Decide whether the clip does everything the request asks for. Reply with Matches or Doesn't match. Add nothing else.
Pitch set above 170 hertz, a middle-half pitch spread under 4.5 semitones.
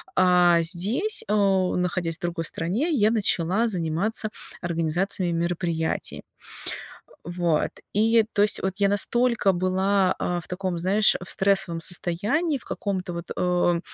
Matches